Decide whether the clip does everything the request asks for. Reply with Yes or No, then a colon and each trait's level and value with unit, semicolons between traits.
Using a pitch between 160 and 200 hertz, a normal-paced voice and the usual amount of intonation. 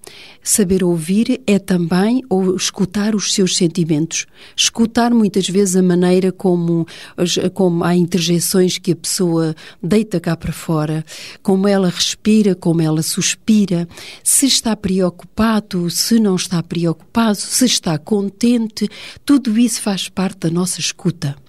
Yes: medium, 185 Hz; average, 135 wpm; average, 3.4 semitones